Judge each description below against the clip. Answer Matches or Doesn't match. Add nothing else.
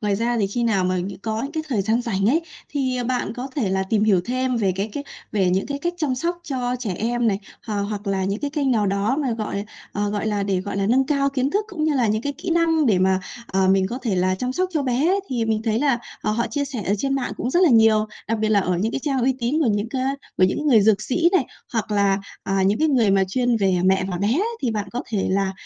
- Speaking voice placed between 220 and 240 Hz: Matches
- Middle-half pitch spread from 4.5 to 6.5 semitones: Matches